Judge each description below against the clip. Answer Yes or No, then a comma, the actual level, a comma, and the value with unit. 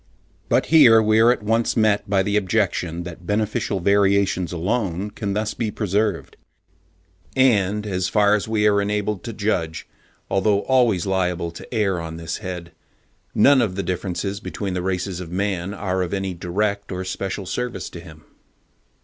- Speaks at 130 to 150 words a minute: No, average, 165 wpm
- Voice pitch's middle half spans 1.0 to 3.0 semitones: Yes, average, 2.7 semitones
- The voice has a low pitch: Yes, low, 100 Hz